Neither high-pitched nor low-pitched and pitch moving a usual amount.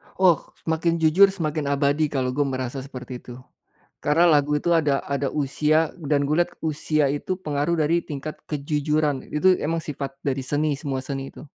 No: medium, 150 Hz; narrow, 2.3 semitones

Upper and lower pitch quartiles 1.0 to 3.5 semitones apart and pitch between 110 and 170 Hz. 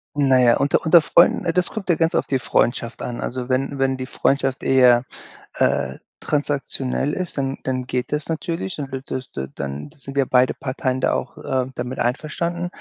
Yes: average, 2.8 semitones; low, 135 Hz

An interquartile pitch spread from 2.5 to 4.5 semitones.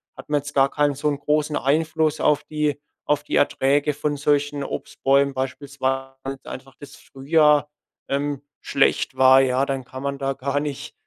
No: narrow, 1.5 semitones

